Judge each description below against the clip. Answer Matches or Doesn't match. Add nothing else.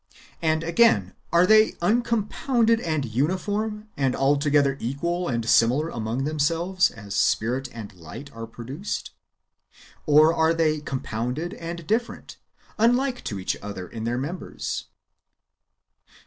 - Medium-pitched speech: Matches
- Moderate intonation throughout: Doesn't match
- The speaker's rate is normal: Doesn't match